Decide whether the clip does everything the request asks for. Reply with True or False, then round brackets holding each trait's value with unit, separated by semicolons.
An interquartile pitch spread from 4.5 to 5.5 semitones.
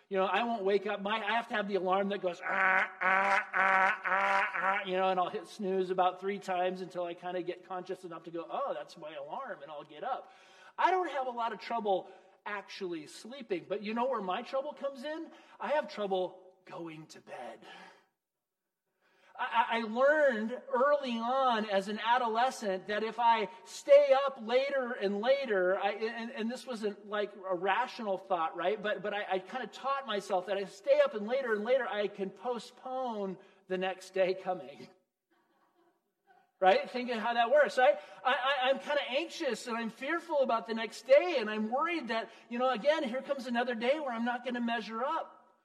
True (4.9 semitones)